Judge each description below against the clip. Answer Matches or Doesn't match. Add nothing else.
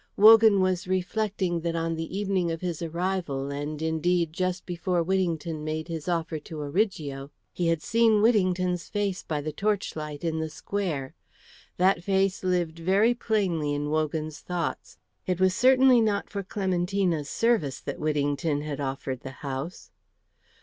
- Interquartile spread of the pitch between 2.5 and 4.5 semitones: Matches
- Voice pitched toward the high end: Doesn't match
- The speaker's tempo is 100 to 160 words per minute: Matches